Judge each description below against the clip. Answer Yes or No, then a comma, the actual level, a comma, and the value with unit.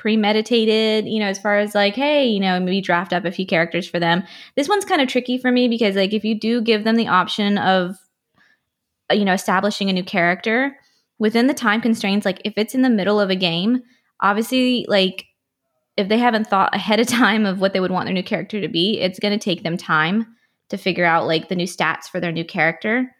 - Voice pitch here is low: No, high, 205 Hz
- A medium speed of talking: No, fast, 235 wpm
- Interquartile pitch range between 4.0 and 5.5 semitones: No, average, 3.6 semitones